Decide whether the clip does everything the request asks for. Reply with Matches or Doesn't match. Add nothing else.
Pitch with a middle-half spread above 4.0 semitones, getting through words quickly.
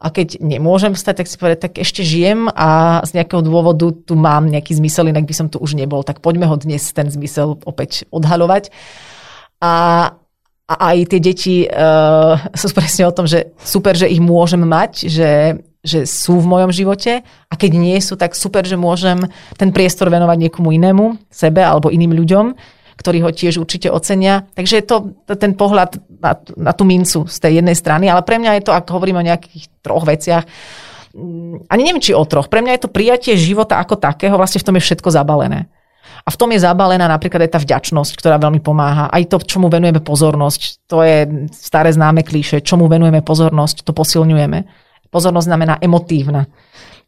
Doesn't match